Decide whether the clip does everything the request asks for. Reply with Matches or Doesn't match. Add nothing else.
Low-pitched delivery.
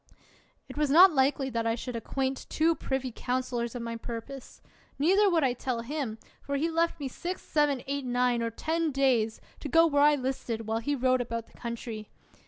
Doesn't match